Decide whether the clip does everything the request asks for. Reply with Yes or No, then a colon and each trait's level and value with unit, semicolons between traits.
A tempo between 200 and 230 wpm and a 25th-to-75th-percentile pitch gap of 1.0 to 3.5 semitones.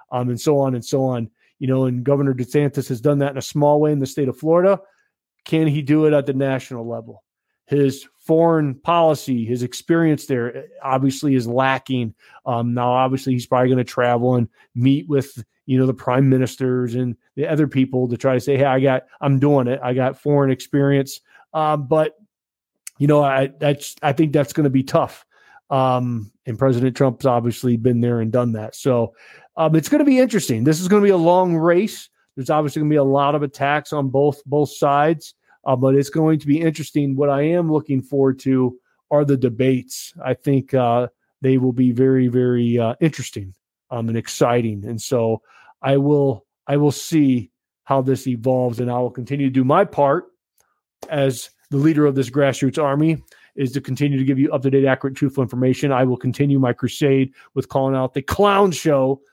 Yes: fast, 205 wpm; narrow, 2.6 semitones